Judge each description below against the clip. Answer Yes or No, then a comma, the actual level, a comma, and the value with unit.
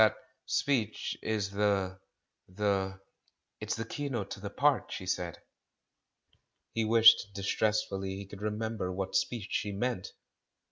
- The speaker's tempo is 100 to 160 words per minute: Yes, average, 140 wpm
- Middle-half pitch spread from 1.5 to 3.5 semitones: Yes, narrow, 2.4 semitones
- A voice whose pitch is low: Yes, low, 105 Hz